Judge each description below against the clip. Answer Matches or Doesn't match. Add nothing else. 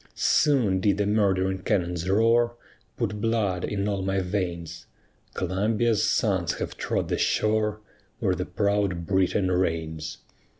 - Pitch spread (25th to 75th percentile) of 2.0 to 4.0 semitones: Matches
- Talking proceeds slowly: Matches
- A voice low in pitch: Matches